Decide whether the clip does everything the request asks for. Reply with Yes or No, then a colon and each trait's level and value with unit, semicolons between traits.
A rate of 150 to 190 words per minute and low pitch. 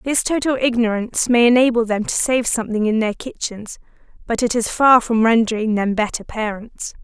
No: average, 180 wpm; high, 230 Hz